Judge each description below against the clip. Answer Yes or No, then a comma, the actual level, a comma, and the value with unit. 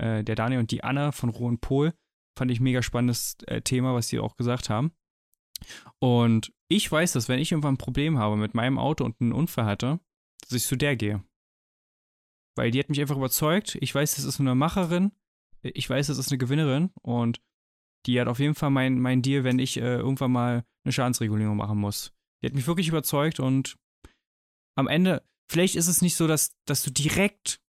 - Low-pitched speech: Yes, low, 130 Hz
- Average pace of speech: No, fast, 205 wpm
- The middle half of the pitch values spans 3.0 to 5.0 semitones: Yes, average, 3.6 semitones